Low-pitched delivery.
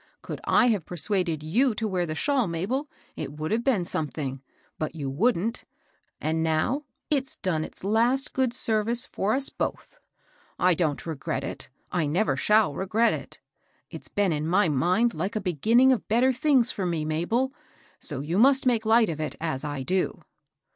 No: high, 190 Hz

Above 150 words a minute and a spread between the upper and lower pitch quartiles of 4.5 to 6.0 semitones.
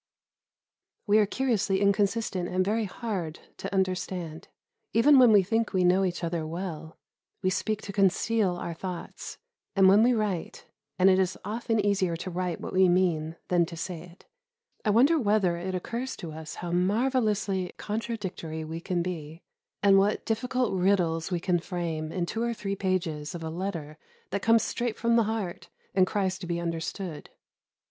No: average, 175 wpm; average, 3.5 semitones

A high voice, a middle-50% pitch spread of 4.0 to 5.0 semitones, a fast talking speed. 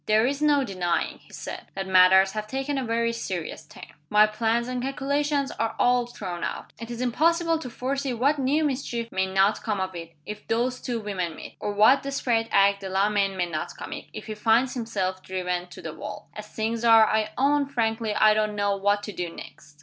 Yes: high, 220 Hz; average, 4.6 semitones; fast, 210 wpm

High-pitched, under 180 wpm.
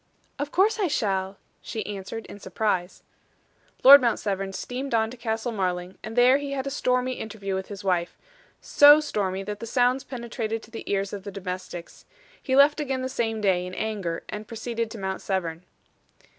No: high, 220 Hz; average, 185 wpm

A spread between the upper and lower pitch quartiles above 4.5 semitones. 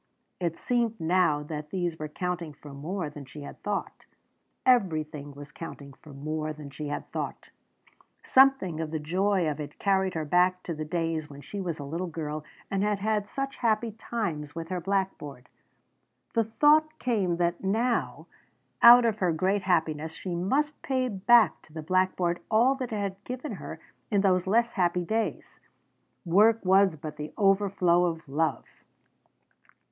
Yes: average, 5.1 semitones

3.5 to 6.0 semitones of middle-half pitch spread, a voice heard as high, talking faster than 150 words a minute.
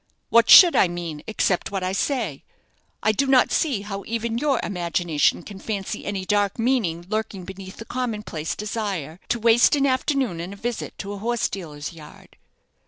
Yes: average, 4.6 semitones; high, 205 Hz; average, 180 wpm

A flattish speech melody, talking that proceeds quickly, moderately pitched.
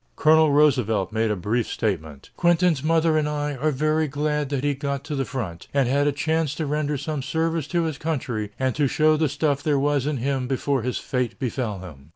No: average, 3.3 semitones; fast, 215 wpm; medium, 145 Hz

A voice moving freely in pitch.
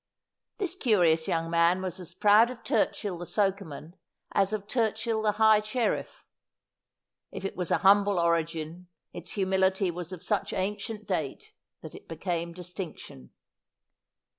No: average, 3.6 semitones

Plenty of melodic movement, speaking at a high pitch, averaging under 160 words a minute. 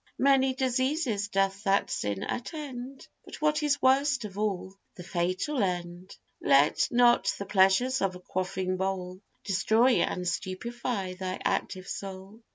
Yes: wide, 5.7 semitones; high, 200 Hz; average, 140 wpm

